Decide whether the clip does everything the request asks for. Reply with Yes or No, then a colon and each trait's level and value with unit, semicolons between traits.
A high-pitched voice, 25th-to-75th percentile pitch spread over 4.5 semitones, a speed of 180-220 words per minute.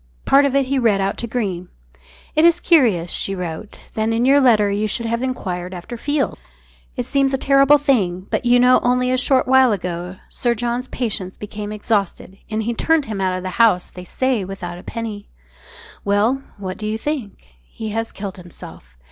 Yes: high, 220 Hz; average, 4.9 semitones; average, 200 wpm